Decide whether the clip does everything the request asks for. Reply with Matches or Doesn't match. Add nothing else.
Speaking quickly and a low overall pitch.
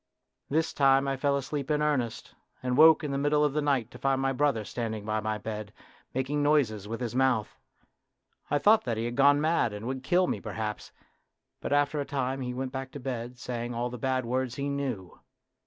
Matches